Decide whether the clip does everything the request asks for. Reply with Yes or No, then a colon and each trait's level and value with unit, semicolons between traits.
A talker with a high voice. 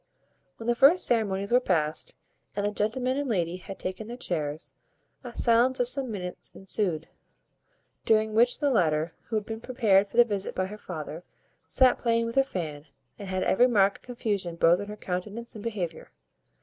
Yes: high, 210 Hz